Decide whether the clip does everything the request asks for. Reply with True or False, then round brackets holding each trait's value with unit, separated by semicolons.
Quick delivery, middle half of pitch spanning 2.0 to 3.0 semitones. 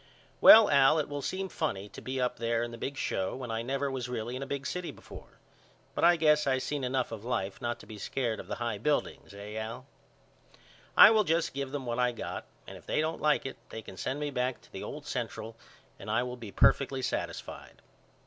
False (235 wpm; 3.7 semitones)